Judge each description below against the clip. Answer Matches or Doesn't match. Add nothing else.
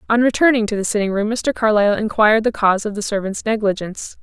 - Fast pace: Matches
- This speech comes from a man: Doesn't match